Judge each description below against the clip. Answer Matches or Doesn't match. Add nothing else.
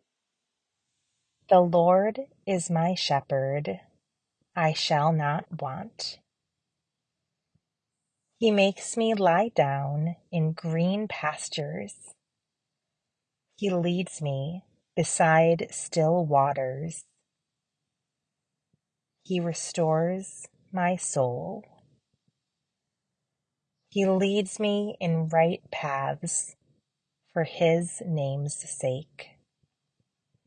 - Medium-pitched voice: Matches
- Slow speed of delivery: Matches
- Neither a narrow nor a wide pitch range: Matches